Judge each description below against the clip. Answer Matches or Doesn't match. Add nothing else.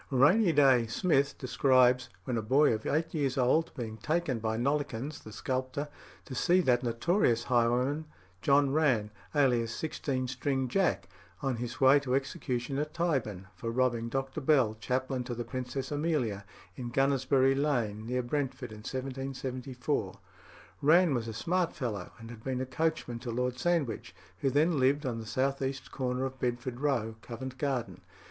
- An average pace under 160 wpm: Doesn't match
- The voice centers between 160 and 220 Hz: Doesn't match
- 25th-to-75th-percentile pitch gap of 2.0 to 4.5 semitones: Matches